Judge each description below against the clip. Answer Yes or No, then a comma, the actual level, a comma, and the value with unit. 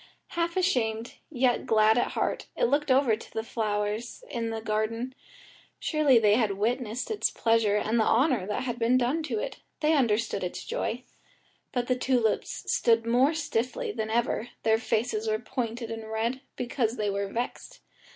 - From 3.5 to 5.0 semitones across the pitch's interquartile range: No, average, 2.8 semitones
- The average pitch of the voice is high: Yes, high, 230 Hz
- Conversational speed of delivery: Yes, average, 175 wpm